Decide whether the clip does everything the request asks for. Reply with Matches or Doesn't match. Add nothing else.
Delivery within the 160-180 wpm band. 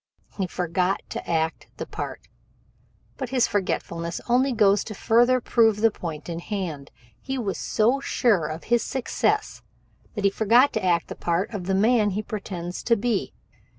Matches